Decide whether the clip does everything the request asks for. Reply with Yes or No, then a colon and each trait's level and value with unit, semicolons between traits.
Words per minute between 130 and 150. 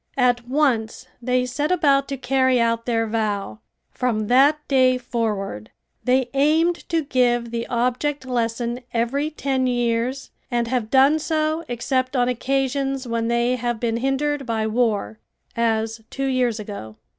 Yes: average, 145 wpm